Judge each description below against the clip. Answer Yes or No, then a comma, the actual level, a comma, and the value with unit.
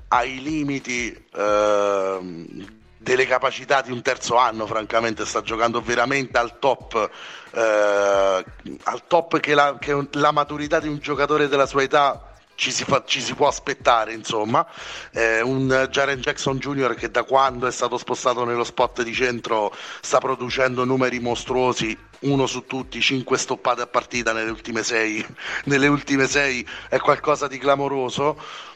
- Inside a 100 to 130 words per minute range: No, average, 150 wpm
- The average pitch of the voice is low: Yes, low, 130 Hz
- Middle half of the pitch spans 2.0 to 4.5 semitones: Yes, average, 3.1 semitones